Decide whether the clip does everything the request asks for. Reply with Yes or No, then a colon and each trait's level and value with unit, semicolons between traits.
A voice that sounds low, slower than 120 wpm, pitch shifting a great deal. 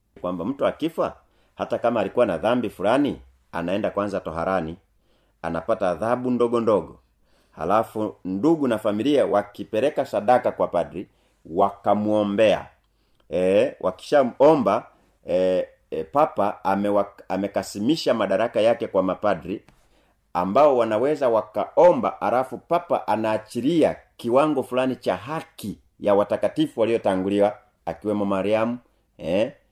No: low, 105 Hz; slow, 100 wpm; average, 3.7 semitones